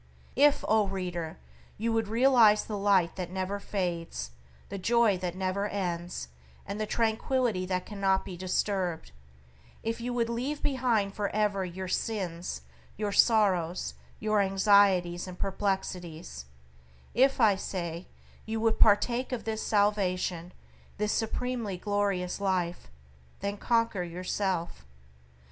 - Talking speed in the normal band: No, slow, 125 wpm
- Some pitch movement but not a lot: Yes, average, 3.3 semitones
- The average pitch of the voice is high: Yes, high, 200 Hz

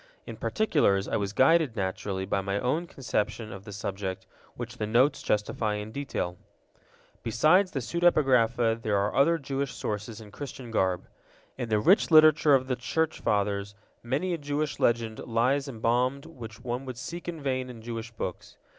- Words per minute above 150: Yes, average, 170 wpm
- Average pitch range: Yes, average, 5.0 semitones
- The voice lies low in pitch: Yes, low, 120 Hz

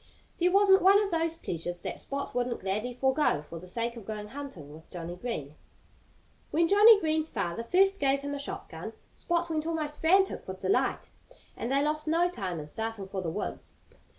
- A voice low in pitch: No, very high, 275 Hz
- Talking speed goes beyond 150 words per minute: Yes, average, 190 wpm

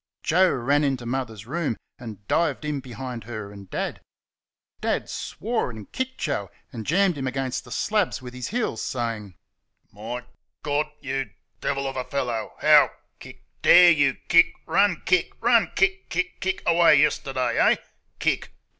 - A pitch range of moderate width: No, wide, 6.1 semitones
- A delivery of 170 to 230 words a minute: No, average, 155 wpm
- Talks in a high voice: No, low, 135 Hz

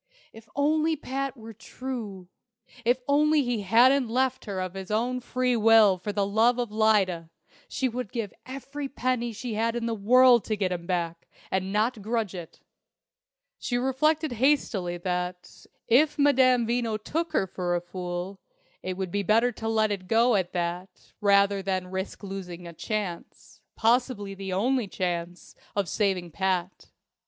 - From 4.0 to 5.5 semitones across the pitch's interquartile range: Yes, average, 4.8 semitones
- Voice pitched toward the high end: Yes, high, 215 Hz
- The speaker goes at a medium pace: Yes, average, 160 wpm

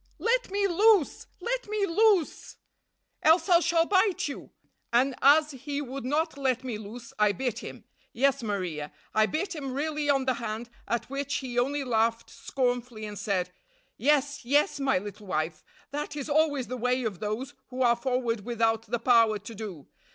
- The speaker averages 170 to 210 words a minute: Yes, average, 175 wpm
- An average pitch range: Yes, average, 4.7 semitones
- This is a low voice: No, very high, 255 Hz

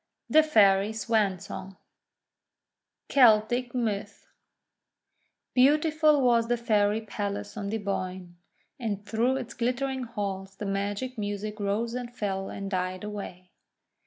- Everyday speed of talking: No, slow, 120 wpm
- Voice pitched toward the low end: No, high, 215 Hz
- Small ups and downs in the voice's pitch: No, average, 3.4 semitones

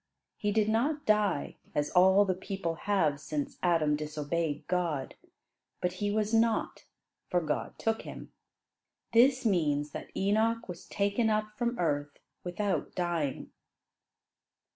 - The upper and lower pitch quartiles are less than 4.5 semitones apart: No, wide, 5.6 semitones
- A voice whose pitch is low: No, medium, 185 Hz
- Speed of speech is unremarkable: No, slow, 130 wpm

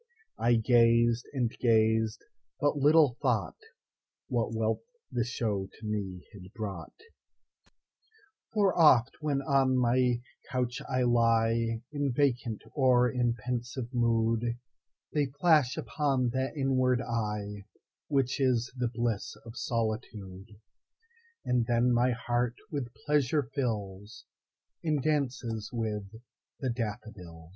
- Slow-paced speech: Yes, slow, 100 wpm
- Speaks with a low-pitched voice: Yes, low, 120 Hz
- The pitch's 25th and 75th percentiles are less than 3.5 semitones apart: Yes, average, 2.9 semitones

